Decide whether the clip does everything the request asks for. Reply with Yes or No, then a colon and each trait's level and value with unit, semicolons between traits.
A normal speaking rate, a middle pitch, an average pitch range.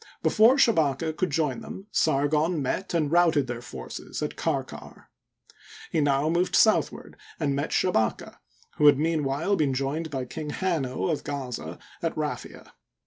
Yes: average, 145 wpm; medium, 150 Hz; average, 3.4 semitones